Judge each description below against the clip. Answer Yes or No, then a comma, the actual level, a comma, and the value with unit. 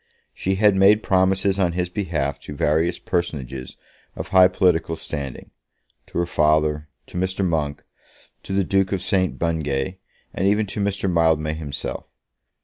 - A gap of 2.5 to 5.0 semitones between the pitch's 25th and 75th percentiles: Yes, average, 3.8 semitones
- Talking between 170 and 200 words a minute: No, average, 150 wpm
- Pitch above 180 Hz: No, very low, 85 Hz